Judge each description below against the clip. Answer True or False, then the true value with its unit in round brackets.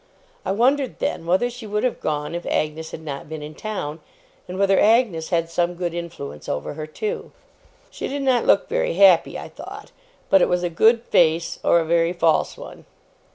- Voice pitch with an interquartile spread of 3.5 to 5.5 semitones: True (4.7 semitones)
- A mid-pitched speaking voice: True (175 Hz)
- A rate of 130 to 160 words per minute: False (200 wpm)